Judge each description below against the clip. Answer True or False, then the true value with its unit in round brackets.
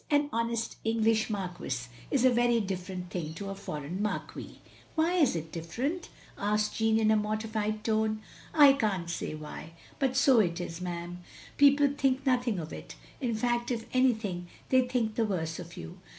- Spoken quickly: False (180 wpm)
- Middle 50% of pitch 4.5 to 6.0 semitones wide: True (5.6 semitones)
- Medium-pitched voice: False (220 Hz)